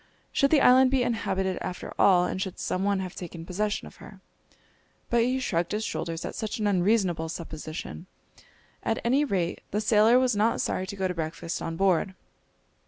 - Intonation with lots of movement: No, average, 4.4 semitones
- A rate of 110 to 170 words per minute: No, average, 185 wpm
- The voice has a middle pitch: No, high, 195 Hz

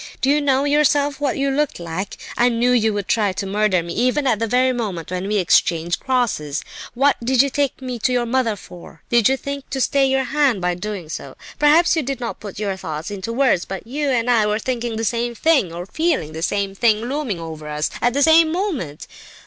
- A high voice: Yes, high, 235 Hz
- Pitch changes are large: Yes, wide, 5.9 semitones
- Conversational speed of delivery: No, fast, 230 wpm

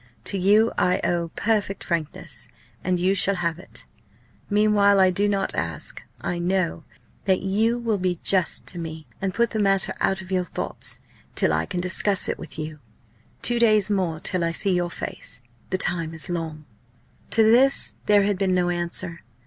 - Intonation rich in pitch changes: No, average, 2.9 semitones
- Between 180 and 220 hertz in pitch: Yes, medium, 185 Hz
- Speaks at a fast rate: No, average, 180 wpm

